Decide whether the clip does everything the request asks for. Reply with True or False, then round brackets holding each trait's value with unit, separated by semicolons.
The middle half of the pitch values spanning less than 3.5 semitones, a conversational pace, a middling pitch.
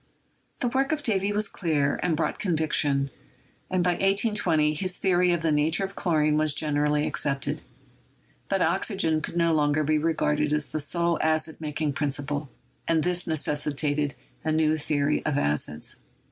True (2.8 semitones; 160 wpm; 155 Hz)